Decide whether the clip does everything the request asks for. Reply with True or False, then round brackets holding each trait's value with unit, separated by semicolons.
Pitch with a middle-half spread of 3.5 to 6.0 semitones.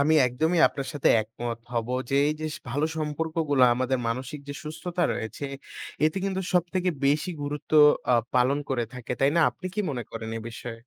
True (4.3 semitones)